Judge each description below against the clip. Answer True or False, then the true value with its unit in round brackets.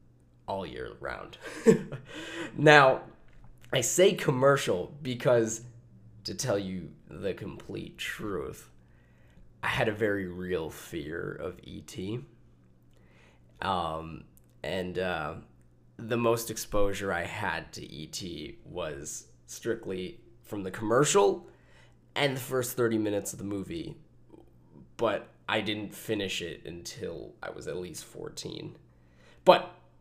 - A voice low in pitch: True (100 Hz)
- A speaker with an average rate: False (115 wpm)